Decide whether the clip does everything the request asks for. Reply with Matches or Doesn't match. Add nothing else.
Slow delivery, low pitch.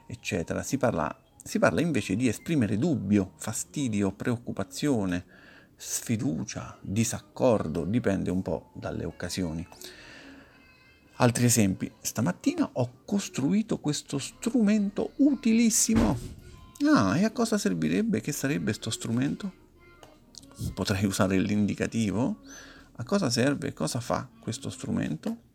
Matches